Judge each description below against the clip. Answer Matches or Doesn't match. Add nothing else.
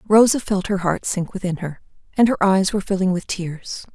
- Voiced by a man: Doesn't match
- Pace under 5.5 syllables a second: Matches